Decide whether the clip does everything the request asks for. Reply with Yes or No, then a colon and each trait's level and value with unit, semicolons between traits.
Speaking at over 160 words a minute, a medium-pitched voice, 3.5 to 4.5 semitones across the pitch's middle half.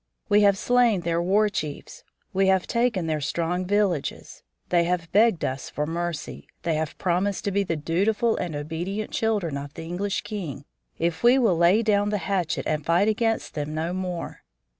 Yes: average, 185 wpm; medium, 180 Hz; average, 4.0 semitones